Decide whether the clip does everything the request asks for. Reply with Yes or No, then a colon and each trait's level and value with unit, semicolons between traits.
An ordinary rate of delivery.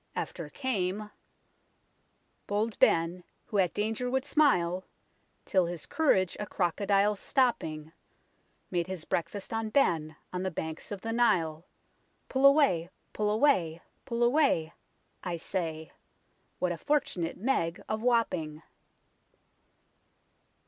No: slow, 120 wpm